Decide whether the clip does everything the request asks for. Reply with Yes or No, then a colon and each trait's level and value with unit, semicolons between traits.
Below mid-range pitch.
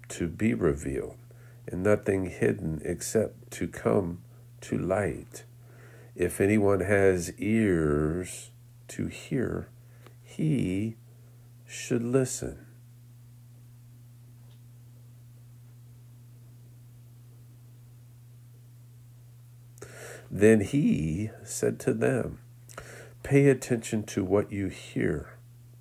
Yes: low, 120 Hz